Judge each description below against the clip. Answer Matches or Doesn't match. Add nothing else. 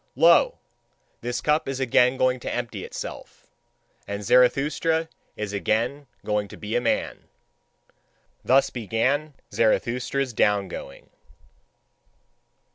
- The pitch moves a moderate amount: Matches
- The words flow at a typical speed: Doesn't match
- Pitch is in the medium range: Doesn't match